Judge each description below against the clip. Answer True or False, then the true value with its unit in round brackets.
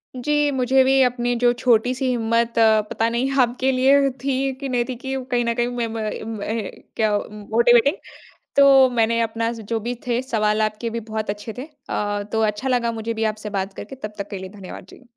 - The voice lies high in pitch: True (235 Hz)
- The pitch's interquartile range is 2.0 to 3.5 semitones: True (2.6 semitones)